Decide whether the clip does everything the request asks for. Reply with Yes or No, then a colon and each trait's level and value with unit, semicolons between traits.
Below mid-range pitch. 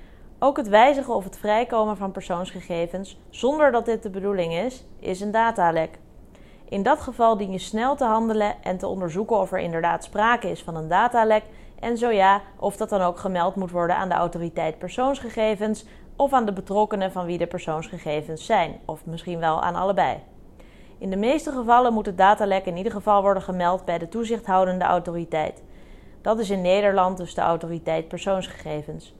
No: high, 195 Hz